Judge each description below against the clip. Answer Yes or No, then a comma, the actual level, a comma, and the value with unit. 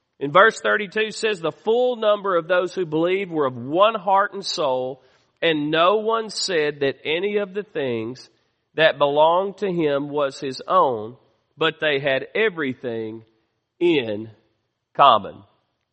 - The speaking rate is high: No, average, 145 wpm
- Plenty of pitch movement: Yes, wide, 7.7 semitones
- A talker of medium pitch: Yes, medium, 155 Hz